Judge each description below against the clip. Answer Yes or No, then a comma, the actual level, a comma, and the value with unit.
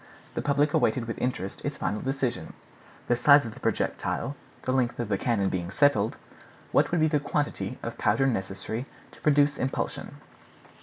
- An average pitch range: Yes, average, 5.0 semitones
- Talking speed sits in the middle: Yes, average, 170 wpm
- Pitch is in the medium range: No, low, 125 Hz